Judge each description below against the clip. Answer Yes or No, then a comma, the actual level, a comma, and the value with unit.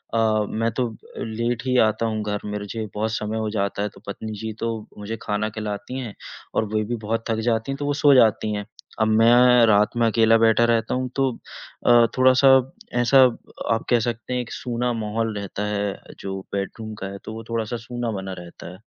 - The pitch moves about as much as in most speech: No, narrow, 2.1 semitones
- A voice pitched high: No, low, 110 Hz